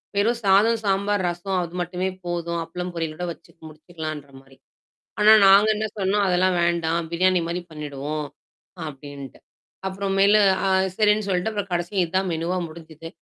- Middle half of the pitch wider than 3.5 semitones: No, average, 3.2 semitones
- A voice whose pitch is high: No, medium, 180 Hz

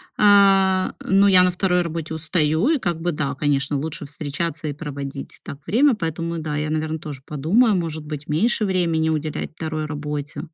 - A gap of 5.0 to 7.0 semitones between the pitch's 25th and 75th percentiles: No, average, 3.4 semitones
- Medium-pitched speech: Yes, medium, 160 Hz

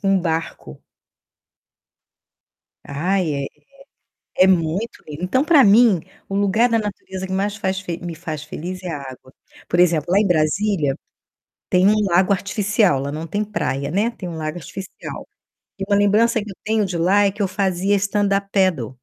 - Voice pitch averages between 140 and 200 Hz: Yes, high, 190 Hz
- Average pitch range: Yes, average, 3.7 semitones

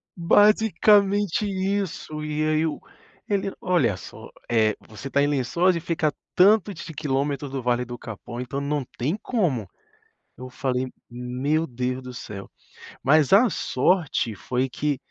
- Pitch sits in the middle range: Yes, medium, 145 Hz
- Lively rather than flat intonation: Yes, wide, 6.3 semitones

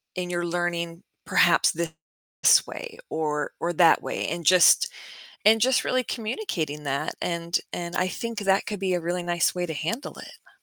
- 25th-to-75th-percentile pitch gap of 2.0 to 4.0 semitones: Yes, average, 2.8 semitones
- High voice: No, medium, 175 Hz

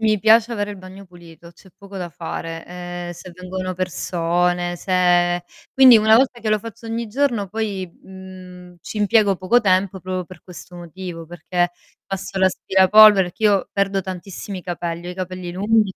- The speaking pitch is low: No, medium, 185 Hz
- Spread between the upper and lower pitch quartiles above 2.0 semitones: Yes, narrow, 2.6 semitones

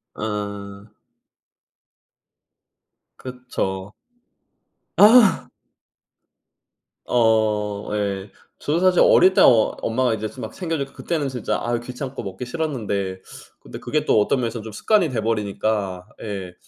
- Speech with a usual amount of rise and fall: Yes, average, 4.4 semitones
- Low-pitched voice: Yes, low, 110 Hz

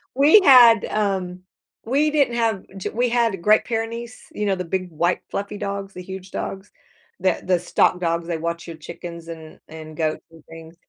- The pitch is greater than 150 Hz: Yes, high, 190 Hz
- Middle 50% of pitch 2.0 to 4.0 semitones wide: No, average, 5.0 semitones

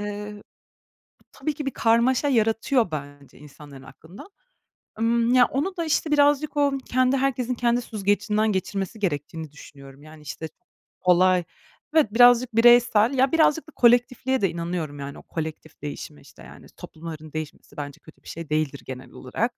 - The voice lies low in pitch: No, high, 210 Hz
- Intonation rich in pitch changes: Yes, wide, 8.2 semitones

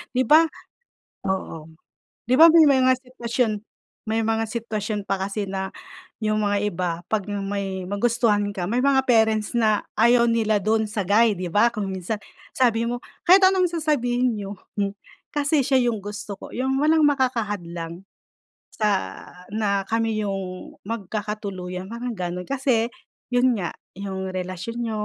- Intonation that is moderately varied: Yes, average, 3.7 semitones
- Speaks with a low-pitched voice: No, high, 215 Hz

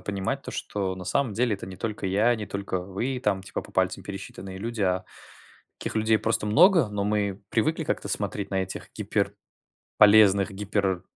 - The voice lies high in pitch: No, low, 100 Hz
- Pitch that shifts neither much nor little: No, narrow, 2.3 semitones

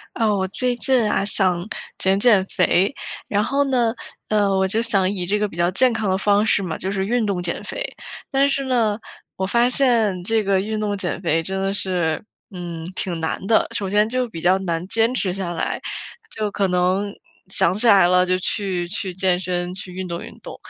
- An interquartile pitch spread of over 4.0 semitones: No, average, 3.2 semitones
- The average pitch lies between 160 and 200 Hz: Yes, high, 195 Hz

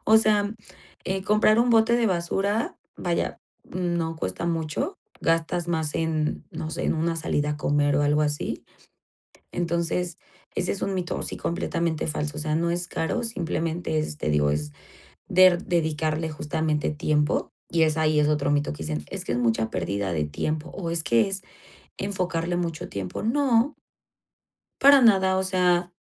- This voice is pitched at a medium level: Yes, medium, 165 Hz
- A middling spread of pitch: Yes, average, 3.5 semitones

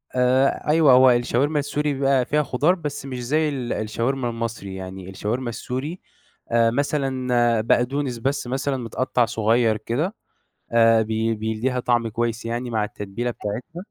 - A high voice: No, low, 120 Hz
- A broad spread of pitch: No, average, 3.1 semitones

